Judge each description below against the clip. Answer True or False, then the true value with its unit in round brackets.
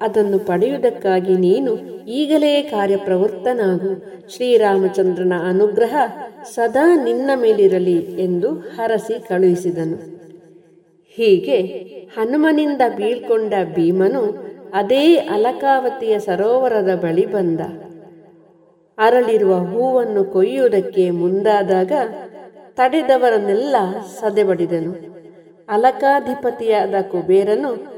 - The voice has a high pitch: True (205 Hz)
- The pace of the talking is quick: False (65 wpm)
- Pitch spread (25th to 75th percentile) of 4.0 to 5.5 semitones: True (5.1 semitones)